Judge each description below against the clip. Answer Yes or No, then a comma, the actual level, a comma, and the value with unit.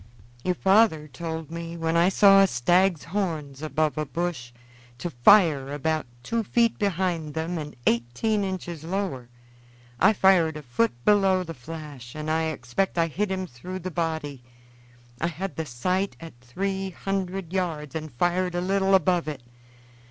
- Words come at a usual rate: Yes, average, 160 wpm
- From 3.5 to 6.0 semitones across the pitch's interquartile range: Yes, average, 3.9 semitones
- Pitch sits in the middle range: Yes, medium, 170 Hz